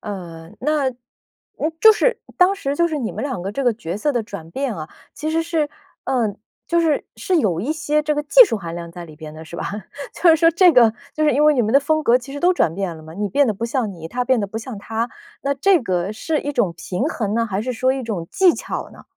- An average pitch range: No, wide, 7.3 semitones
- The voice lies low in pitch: No, high, 245 Hz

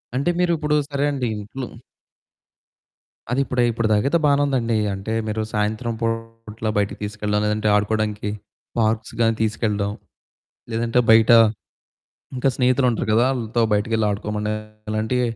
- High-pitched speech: No, low, 115 Hz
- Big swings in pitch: No, average, 2.7 semitones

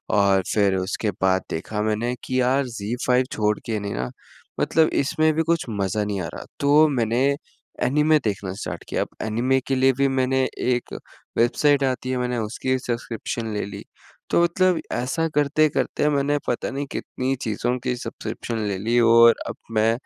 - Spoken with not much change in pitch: No, average, 4.4 semitones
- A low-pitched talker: Yes, low, 125 Hz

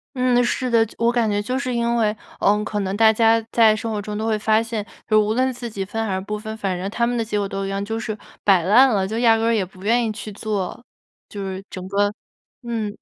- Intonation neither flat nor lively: No, narrow, 2.3 semitones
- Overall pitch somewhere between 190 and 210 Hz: No, high, 220 Hz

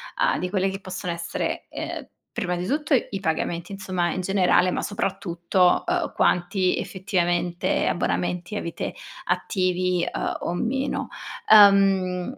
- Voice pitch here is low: No, medium, 185 Hz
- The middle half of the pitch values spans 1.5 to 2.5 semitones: Yes, narrow, 2.1 semitones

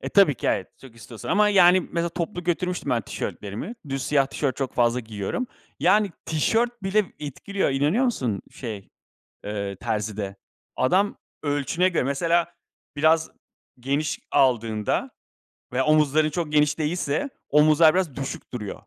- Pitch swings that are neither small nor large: No, wide, 5.9 semitones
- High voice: No, medium, 150 Hz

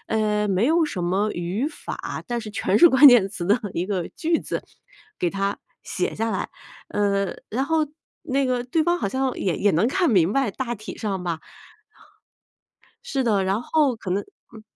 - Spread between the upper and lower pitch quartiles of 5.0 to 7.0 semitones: Yes, average, 5.3 semitones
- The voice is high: Yes, high, 215 Hz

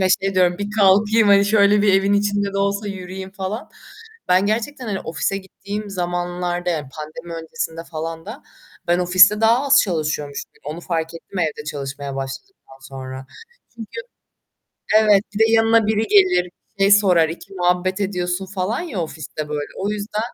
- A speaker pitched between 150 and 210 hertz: Yes, high, 190 Hz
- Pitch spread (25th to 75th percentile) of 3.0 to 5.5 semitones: Yes, average, 3.7 semitones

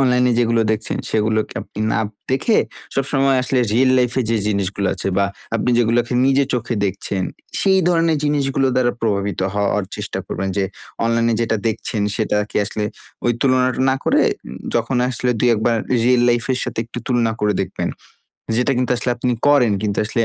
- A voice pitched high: No, low, 120 Hz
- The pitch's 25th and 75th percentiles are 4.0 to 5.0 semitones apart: No, average, 2.9 semitones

